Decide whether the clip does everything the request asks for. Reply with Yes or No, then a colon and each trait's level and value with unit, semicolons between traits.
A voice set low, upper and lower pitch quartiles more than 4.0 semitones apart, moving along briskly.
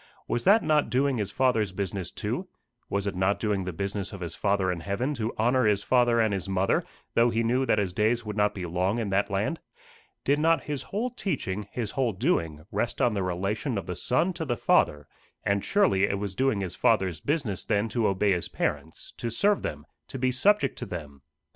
Yes: low, 105 Hz; average, 4.9 semitones; fast, 215 wpm